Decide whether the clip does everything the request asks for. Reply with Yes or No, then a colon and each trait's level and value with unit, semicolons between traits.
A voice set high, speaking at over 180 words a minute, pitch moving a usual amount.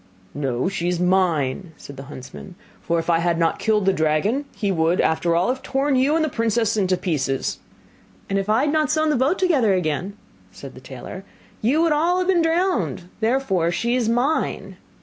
No: high, 195 Hz; average, 200 wpm; wide, 8.2 semitones